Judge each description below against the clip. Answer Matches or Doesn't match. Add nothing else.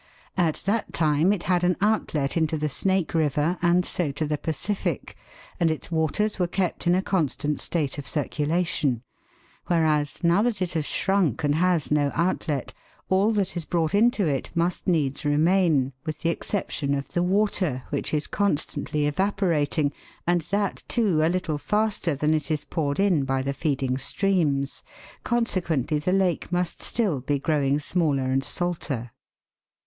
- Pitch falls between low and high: Matches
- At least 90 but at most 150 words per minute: Doesn't match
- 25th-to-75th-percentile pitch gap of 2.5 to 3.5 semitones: Doesn't match